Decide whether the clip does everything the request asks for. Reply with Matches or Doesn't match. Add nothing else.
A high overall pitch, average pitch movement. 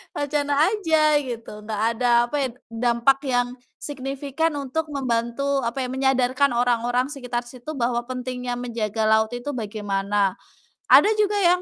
Matches